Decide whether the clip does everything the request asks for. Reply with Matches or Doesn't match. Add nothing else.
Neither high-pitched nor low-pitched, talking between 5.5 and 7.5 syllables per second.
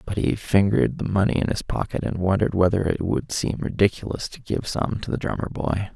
Doesn't match